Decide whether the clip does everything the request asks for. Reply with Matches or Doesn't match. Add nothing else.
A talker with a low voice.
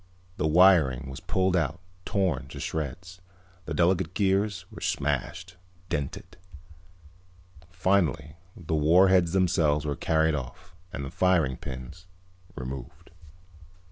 Matches